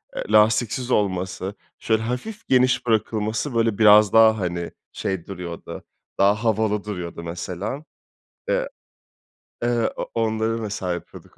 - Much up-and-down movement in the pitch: No, average, 3.2 semitones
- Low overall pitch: Yes, low, 110 Hz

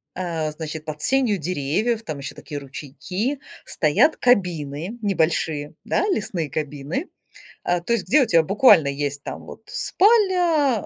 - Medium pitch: Yes, medium, 170 Hz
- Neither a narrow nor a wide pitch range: No, wide, 8.1 semitones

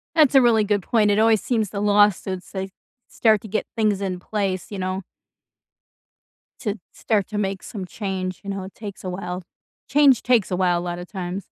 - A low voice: No, high, 200 Hz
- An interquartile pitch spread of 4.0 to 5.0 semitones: No, narrow, 2.6 semitones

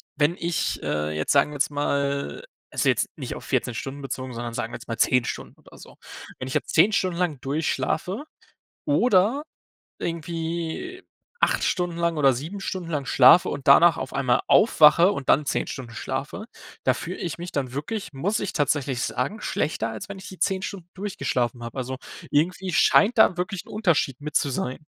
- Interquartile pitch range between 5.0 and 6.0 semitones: Yes, average, 5.3 semitones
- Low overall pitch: No, medium, 155 Hz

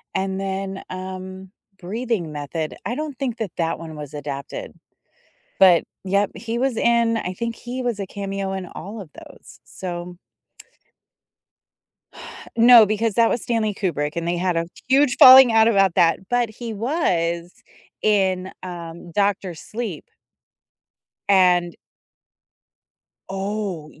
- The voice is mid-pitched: No, high, 195 Hz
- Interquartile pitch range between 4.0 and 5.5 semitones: Yes, average, 4.6 semitones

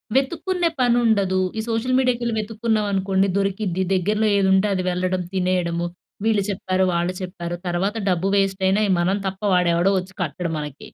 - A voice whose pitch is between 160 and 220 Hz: Yes, high, 190 Hz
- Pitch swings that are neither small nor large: Yes, average, 3.1 semitones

